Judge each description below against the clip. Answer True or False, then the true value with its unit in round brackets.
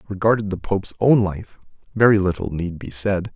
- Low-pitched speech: True (95 Hz)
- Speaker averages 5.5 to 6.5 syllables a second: True (5.7 syllables/s)